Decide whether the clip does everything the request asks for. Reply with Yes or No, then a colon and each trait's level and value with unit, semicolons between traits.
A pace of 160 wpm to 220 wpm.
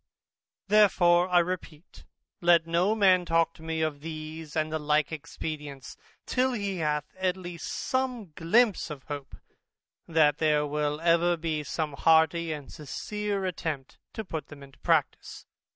No: average, 150 wpm